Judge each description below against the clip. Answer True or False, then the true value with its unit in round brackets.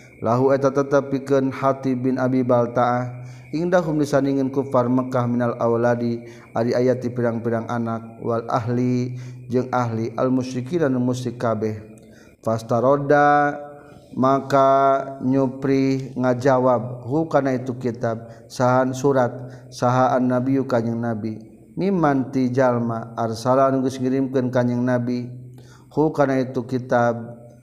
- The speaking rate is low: False (110 wpm)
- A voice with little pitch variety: True (2.0 semitones)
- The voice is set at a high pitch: False (125 Hz)